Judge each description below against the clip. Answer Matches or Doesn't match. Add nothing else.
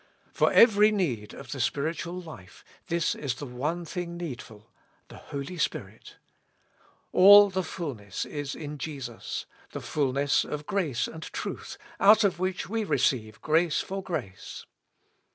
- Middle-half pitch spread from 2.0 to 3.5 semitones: Doesn't match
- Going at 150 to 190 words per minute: Doesn't match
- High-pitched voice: Doesn't match